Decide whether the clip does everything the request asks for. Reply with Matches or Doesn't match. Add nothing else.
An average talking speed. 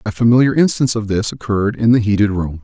Doesn't match